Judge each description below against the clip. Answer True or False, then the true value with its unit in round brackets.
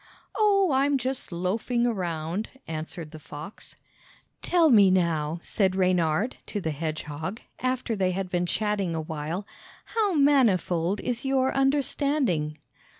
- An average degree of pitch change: False (7.8 semitones)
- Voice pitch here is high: True (195 Hz)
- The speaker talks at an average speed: False (130 wpm)